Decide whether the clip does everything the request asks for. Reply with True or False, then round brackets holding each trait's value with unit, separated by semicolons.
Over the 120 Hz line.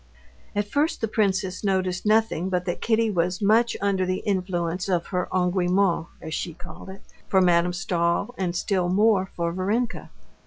True (185 Hz)